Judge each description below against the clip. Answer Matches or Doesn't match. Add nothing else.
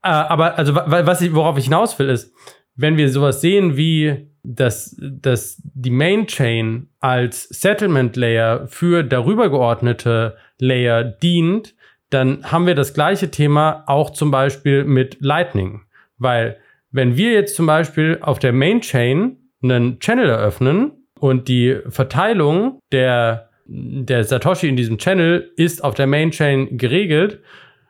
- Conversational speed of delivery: Matches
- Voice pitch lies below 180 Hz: Matches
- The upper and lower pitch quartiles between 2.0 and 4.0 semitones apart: Doesn't match